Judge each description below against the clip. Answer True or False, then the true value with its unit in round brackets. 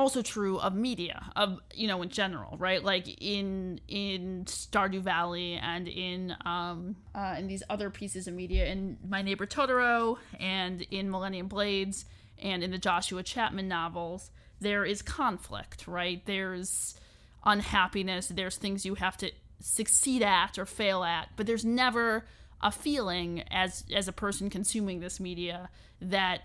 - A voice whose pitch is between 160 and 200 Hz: True (190 Hz)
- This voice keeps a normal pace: True (155 wpm)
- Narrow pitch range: True (1.9 semitones)